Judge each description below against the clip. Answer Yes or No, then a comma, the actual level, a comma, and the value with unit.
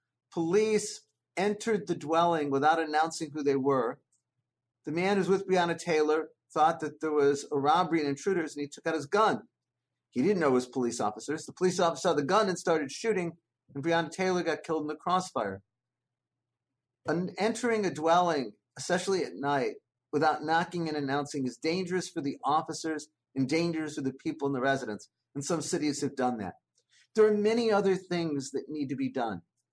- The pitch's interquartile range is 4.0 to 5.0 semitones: Yes, average, 4.5 semitones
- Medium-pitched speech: Yes, medium, 155 Hz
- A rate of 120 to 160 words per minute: No, average, 190 wpm